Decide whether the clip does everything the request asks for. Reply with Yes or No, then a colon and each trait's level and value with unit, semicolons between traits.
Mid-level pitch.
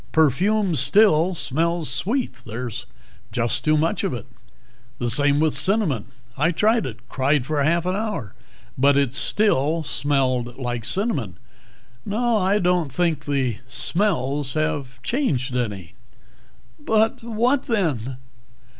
Yes: medium, 150 Hz